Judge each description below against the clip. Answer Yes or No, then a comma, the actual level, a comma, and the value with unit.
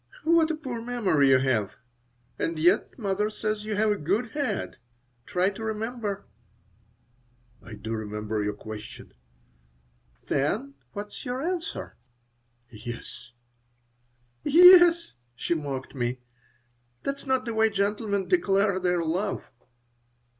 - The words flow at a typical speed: No, slow, 120 wpm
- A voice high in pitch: Yes, high, 205 Hz